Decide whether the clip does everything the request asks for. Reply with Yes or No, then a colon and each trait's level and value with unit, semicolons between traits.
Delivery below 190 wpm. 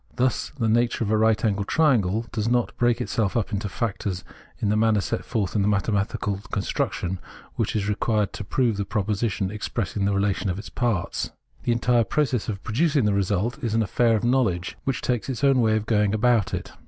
No: fast, 205 wpm